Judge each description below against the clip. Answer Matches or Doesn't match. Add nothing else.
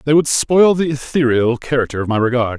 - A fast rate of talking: Matches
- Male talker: Matches